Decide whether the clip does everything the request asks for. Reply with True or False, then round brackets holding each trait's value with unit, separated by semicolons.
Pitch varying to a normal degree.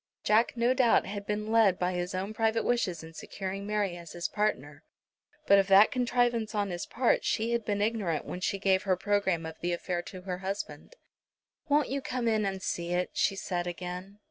True (3.7 semitones)